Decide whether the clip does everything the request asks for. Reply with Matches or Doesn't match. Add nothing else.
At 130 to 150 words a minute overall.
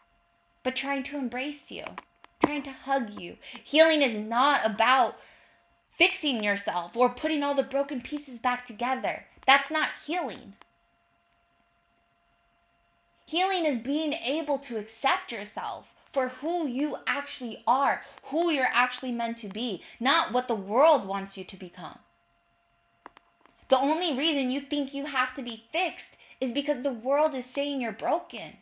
Matches